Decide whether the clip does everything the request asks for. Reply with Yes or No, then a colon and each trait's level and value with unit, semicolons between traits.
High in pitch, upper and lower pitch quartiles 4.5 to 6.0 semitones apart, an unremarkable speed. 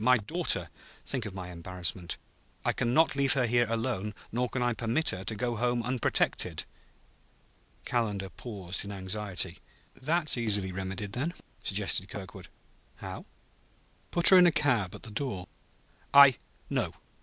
No: low, 115 Hz; average, 5.1 semitones; average, 150 wpm